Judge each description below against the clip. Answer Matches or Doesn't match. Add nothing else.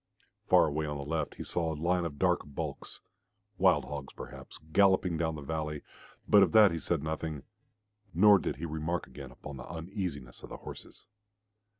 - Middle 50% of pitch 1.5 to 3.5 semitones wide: Matches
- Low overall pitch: Matches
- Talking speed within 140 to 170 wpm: Doesn't match